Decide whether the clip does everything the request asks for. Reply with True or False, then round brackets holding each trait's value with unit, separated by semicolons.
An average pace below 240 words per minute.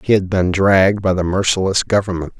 True (200 wpm)